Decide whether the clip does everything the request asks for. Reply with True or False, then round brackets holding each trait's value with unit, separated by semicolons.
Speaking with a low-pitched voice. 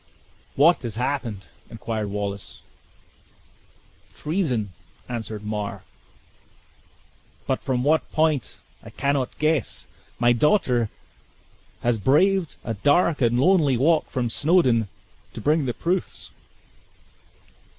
True (130 Hz)